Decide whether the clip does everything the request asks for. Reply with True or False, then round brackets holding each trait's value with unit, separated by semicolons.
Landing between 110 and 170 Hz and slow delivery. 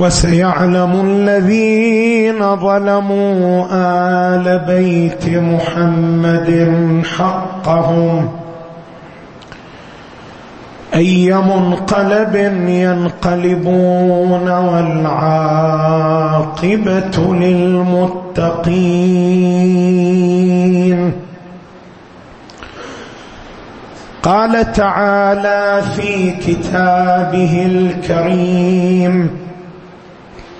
False (180 Hz; 35 wpm)